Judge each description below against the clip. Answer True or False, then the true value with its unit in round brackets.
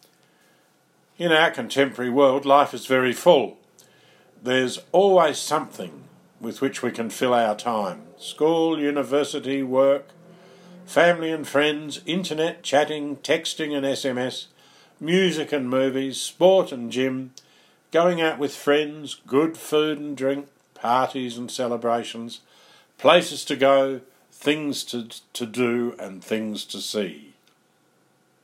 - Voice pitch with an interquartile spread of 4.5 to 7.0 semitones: False (3.3 semitones)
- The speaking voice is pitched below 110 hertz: False (140 Hz)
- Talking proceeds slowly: True (120 wpm)